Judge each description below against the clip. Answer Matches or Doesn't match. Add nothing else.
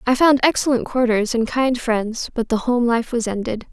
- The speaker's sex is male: Doesn't match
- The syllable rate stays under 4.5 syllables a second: Doesn't match